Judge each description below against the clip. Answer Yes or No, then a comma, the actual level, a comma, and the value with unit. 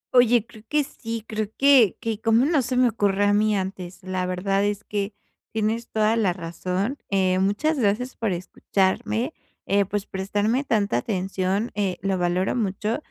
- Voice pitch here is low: No, high, 205 Hz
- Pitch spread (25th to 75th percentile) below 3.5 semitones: Yes, average, 3.1 semitones